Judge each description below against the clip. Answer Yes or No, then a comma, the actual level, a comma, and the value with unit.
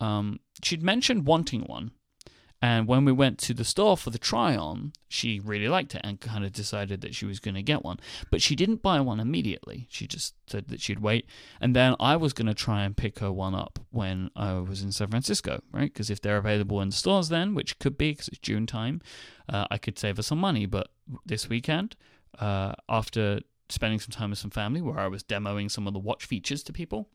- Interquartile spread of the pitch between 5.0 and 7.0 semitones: Yes, wide, 5.4 semitones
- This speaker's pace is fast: Yes, fast, 235 wpm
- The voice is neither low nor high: No, low, 110 Hz